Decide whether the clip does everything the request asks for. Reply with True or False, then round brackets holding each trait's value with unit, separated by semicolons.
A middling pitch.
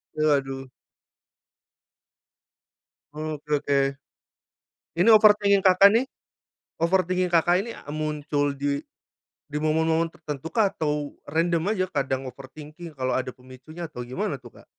True (155 Hz)